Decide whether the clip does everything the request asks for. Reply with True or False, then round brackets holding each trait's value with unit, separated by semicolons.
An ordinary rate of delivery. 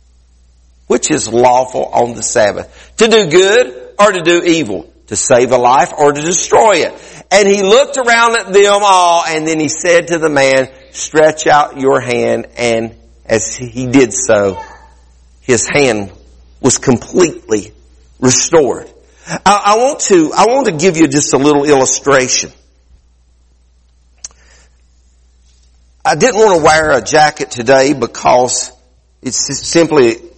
True (145 wpm)